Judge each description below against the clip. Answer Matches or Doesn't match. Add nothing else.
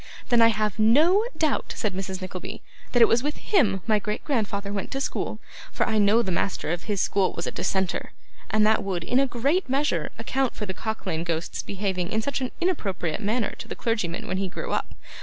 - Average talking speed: Doesn't match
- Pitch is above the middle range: Matches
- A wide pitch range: Doesn't match